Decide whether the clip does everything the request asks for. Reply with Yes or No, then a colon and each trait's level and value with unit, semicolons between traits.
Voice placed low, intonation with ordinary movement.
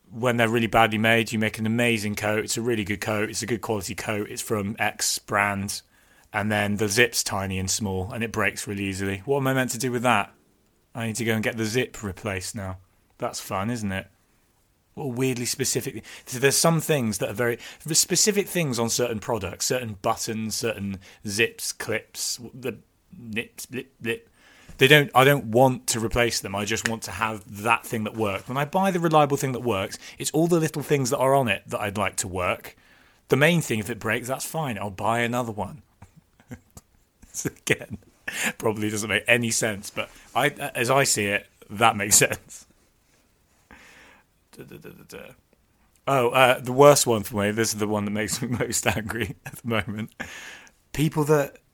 Yes: low, 115 Hz; average, 3.6 semitones